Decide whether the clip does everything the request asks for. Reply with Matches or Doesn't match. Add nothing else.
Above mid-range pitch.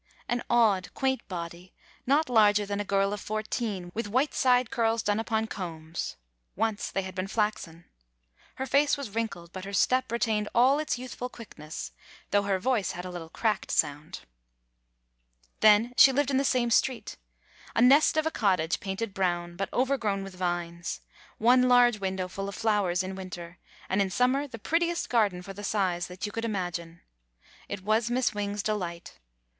Matches